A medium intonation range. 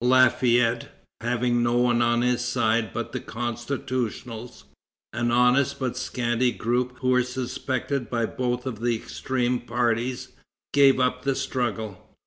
No: narrow, 1.2 semitones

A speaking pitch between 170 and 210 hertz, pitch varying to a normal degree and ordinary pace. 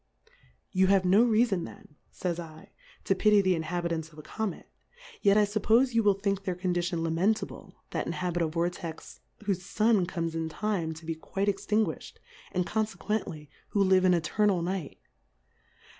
Yes: medium, 185 Hz; average, 3.6 semitones; average, 165 wpm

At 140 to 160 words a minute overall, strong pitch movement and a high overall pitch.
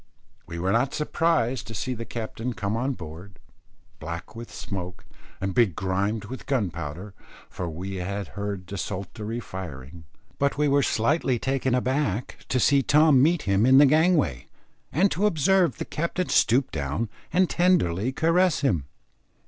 No: average, 150 wpm; wide, 6.9 semitones; low, 115 Hz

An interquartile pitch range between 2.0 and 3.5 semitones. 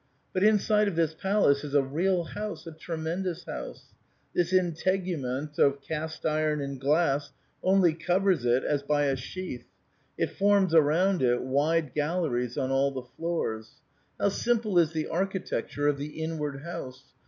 No: average, 4.6 semitones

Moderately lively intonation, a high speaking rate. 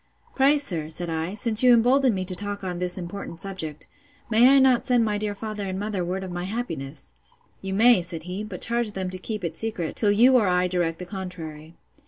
Yes: average, 4.0 semitones; fast, 220 wpm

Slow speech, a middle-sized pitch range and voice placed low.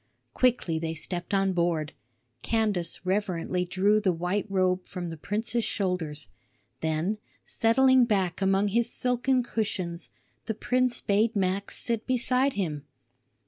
No: slow, 130 wpm; average, 4.4 semitones; high, 195 Hz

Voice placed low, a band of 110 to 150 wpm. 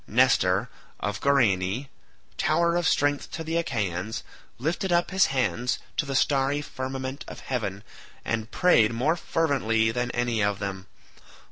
Yes: low, 130 Hz; average, 140 wpm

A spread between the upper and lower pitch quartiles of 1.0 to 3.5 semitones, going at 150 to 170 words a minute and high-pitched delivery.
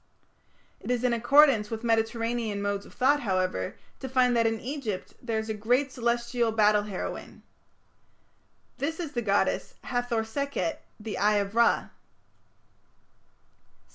No: average, 2.9 semitones; average, 140 wpm; high, 230 Hz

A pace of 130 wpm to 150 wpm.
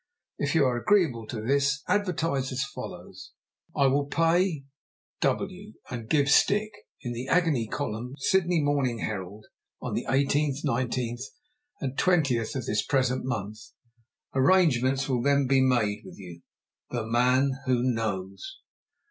Yes: average, 140 wpm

